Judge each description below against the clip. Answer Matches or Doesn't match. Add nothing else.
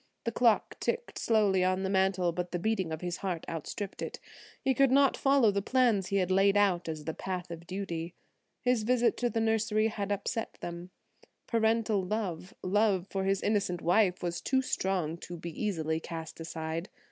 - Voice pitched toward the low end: Doesn't match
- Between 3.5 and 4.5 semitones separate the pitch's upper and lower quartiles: Matches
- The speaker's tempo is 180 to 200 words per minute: Matches